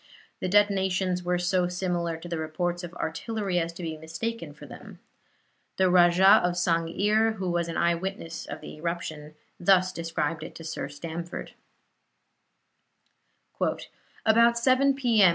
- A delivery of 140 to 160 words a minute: Yes, average, 150 wpm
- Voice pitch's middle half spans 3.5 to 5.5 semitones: No, average, 2.7 semitones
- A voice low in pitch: No, medium, 180 Hz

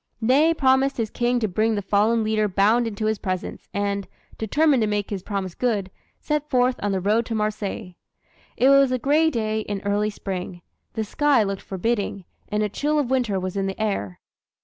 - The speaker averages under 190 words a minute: No, average, 195 wpm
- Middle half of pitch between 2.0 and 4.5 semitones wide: Yes, average, 3.8 semitones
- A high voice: Yes, high, 215 Hz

